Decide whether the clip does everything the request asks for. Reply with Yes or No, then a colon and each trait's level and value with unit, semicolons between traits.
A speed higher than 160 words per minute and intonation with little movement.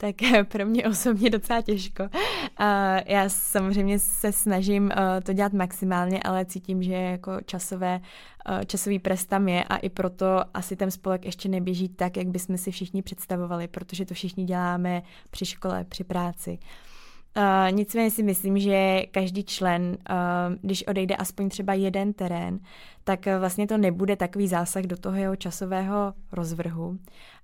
No: average, 145 wpm; narrow, 1.5 semitones